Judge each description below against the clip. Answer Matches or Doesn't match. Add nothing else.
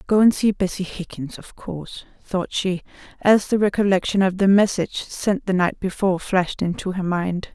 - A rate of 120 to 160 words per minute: Doesn't match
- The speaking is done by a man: Doesn't match